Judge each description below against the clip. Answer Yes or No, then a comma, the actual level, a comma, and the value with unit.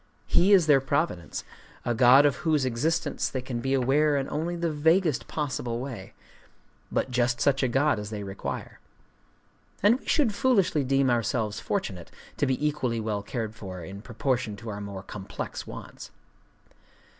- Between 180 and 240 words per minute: No, average, 160 wpm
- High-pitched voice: No, low, 130 Hz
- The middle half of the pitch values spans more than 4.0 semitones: Yes, average, 5.2 semitones